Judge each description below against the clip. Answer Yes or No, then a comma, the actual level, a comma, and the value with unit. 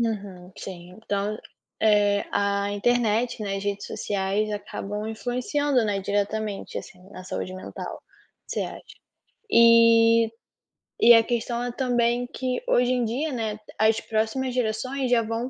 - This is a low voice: No, high, 220 Hz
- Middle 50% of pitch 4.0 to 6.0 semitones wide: No, average, 3.0 semitones